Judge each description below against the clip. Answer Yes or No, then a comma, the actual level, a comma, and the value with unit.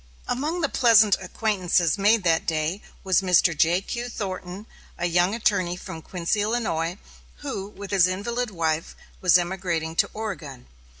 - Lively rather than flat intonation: No, average, 3.8 semitones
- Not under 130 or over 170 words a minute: Yes, average, 140 wpm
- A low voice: No, medium, 185 Hz